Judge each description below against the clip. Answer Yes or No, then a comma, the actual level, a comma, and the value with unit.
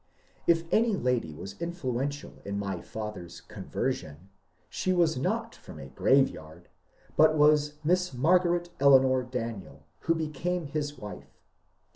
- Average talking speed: No, slow, 125 wpm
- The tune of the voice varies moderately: No, wide, 7.6 semitones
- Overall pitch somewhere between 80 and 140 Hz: Yes, low, 135 Hz